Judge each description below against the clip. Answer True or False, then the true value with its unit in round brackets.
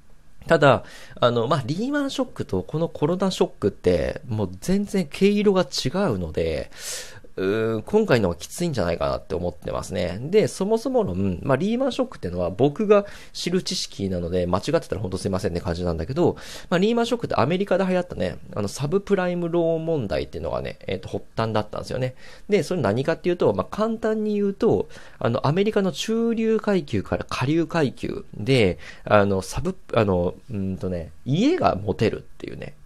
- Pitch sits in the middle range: True (165 Hz)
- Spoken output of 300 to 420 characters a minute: True (415 characters per minute)